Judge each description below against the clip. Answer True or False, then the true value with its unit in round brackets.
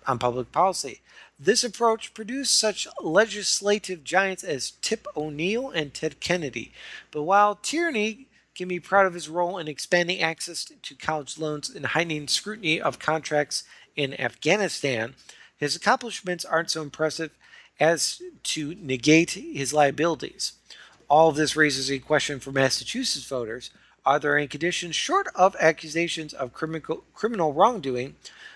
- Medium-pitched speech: True (160 Hz)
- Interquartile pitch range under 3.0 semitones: False (4.7 semitones)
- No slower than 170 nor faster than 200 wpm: False (135 wpm)